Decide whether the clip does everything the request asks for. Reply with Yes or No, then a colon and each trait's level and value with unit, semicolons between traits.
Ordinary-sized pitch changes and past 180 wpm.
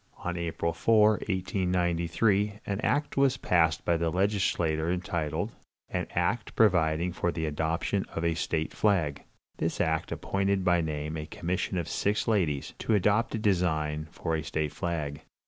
No: average, 3.6 semitones; average, 155 wpm